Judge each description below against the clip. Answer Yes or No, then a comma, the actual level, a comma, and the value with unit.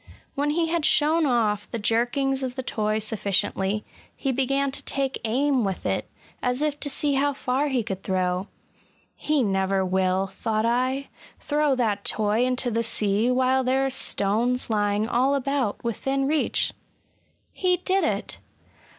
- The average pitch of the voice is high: Yes, very high, 250 Hz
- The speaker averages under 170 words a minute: Yes, average, 160 wpm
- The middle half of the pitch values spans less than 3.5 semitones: No, average, 4.7 semitones